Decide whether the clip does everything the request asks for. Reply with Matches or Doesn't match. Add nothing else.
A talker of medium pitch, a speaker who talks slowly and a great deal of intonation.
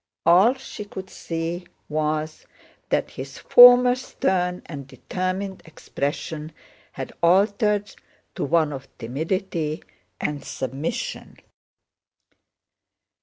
Doesn't match